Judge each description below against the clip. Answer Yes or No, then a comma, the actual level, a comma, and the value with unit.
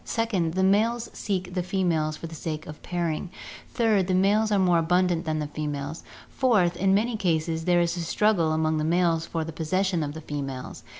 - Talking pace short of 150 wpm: No, average, 200 wpm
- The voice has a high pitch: No, medium, 175 Hz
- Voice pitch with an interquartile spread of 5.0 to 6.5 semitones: No, average, 3.3 semitones